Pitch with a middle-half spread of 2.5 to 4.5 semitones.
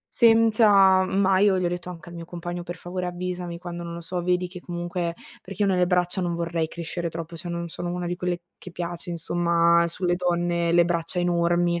No: narrow, 1.0 semitones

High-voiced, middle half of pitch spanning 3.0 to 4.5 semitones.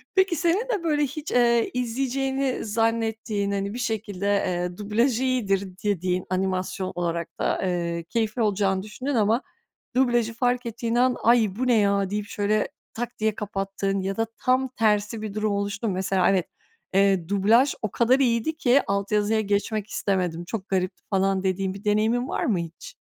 Yes: high, 210 Hz; average, 3.6 semitones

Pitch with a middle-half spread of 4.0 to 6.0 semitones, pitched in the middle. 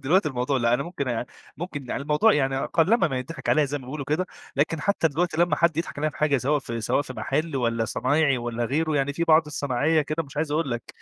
No: average, 3.5 semitones; medium, 145 Hz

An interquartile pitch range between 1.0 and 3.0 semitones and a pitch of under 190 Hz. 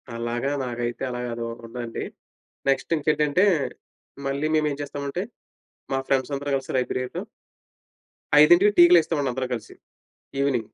No: average, 3.7 semitones; low, 135 Hz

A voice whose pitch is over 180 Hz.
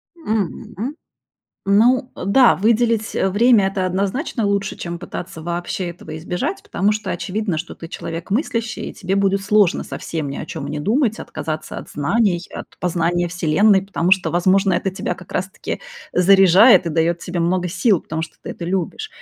Yes: high, 190 Hz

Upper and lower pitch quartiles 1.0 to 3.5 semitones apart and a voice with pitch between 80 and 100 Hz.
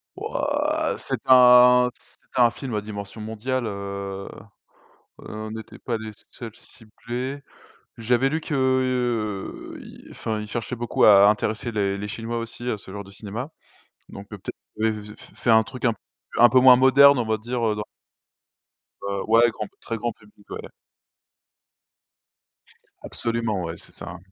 No: average, 2.9 semitones; low, 110 Hz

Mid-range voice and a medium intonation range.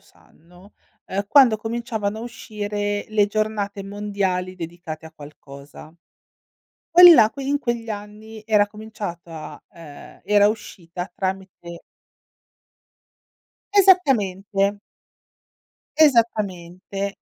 No: high, 205 Hz; average, 3.2 semitones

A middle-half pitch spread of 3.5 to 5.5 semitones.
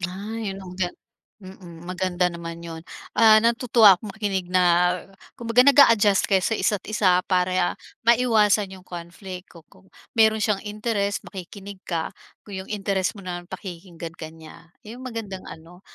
No: average, 3.1 semitones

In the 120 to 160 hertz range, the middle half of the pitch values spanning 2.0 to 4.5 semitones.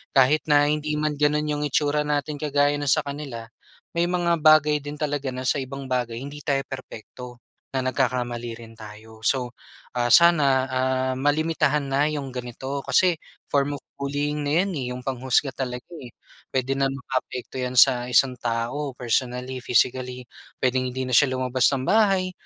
Yes: low, 135 Hz; average, 2.7 semitones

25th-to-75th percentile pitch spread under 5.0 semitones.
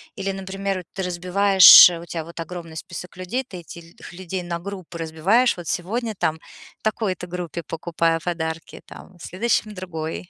Yes: narrow, 2.5 semitones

